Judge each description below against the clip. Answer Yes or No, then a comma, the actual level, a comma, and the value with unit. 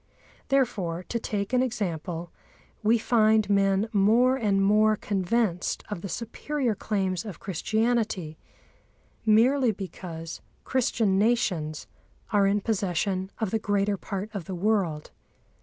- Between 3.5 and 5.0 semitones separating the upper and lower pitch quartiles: No, average, 3.1 semitones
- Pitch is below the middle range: No, high, 205 Hz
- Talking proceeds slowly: Yes, slow, 125 wpm